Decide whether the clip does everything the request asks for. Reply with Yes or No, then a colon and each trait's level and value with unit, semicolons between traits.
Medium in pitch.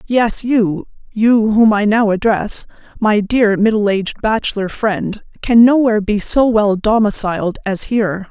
No: high, 215 Hz